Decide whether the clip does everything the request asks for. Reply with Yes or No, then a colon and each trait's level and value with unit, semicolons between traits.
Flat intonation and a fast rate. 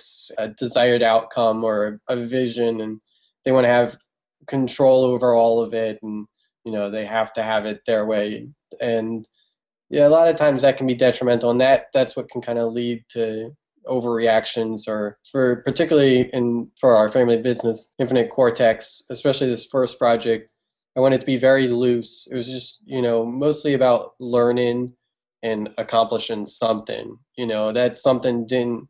No: narrow, 2.2 semitones; average, 170 wpm